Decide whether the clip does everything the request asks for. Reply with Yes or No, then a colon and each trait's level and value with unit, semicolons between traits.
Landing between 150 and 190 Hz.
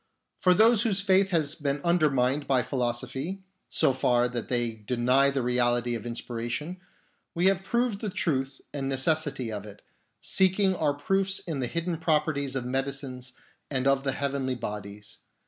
No: low, 135 Hz